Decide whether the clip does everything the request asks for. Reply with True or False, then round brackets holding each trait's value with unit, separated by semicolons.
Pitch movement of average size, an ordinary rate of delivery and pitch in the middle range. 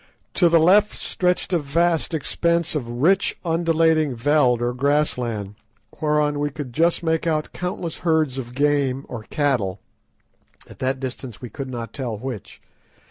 True (4.6 semitones; 155 wpm; 145 Hz)